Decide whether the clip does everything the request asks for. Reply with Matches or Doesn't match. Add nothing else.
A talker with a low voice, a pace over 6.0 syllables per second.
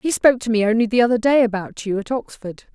Doesn't match